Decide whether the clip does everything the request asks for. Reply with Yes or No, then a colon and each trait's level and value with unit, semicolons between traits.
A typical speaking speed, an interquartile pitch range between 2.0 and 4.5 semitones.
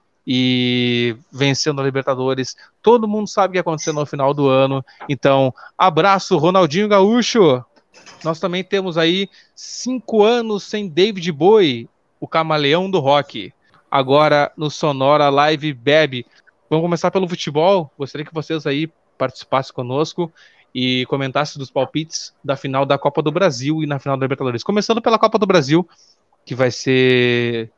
No: average, 150 wpm; average, 5.3 semitones